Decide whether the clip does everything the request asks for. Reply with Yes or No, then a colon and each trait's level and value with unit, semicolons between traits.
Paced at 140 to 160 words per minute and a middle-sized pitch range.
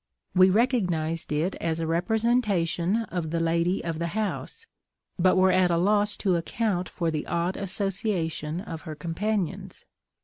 Yes: average, 150 wpm; average, 3.6 semitones